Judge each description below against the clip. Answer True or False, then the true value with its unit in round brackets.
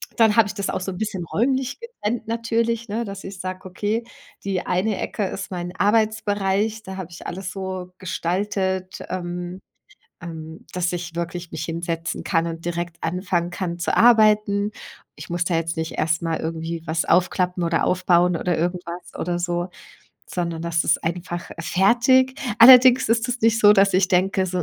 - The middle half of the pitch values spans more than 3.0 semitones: True (3.4 semitones)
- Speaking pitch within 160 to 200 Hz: True (185 Hz)